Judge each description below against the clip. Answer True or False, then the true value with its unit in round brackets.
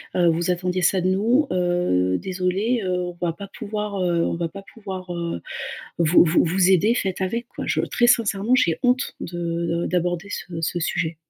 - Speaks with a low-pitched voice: False (180 Hz)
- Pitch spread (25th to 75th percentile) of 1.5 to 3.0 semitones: True (2.7 semitones)